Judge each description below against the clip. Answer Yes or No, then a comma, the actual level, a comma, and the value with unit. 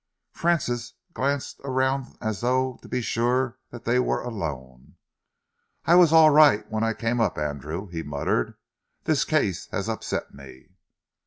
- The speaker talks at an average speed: Yes, average, 150 wpm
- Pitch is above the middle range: No, low, 120 Hz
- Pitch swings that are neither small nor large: No, wide, 7.4 semitones